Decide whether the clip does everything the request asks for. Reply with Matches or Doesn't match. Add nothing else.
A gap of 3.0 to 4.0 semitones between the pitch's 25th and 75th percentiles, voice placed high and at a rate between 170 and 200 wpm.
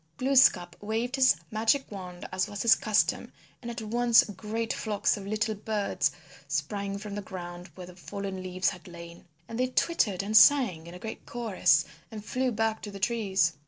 Matches